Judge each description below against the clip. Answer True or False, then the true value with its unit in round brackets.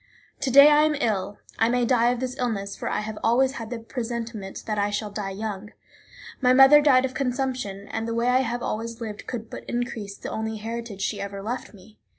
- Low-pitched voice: False (230 Hz)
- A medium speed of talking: False (220 wpm)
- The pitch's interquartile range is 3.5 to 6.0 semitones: False (3.1 semitones)